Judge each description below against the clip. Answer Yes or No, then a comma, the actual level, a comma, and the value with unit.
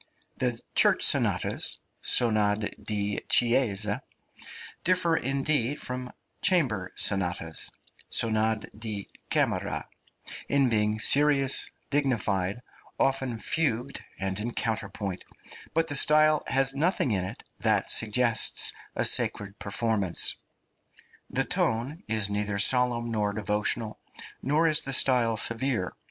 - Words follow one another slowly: Yes, slow, 110 wpm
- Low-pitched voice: Yes, low, 115 Hz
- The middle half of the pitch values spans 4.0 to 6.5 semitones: Yes, average, 4.6 semitones